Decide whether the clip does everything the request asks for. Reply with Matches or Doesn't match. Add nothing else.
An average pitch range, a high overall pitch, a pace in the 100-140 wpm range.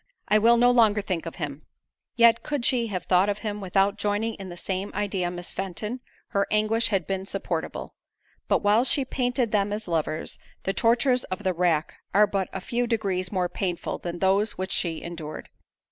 Doesn't match